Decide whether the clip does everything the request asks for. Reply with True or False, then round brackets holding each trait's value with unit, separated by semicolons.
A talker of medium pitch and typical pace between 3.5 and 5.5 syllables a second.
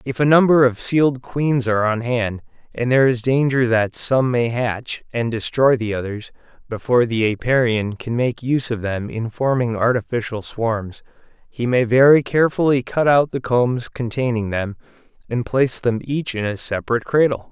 False (120 Hz; 5.0 syllables/s)